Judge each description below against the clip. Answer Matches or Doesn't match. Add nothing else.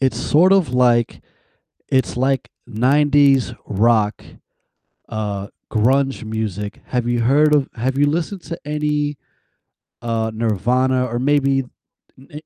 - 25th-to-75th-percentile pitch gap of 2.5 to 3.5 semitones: Doesn't match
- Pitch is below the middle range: Matches